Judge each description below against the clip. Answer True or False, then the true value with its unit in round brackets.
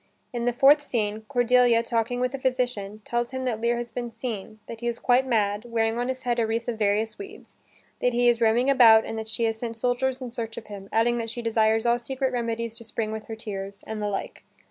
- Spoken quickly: True (245 wpm)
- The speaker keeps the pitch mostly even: True (1.8 semitones)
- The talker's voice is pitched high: True (235 Hz)